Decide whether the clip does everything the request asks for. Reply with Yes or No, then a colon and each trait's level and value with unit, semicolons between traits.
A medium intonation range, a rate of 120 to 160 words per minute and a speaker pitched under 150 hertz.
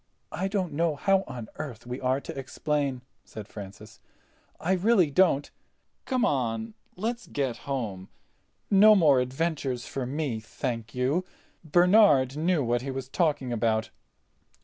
No: wide, 6.0 semitones; slow, 135 wpm; low, 135 Hz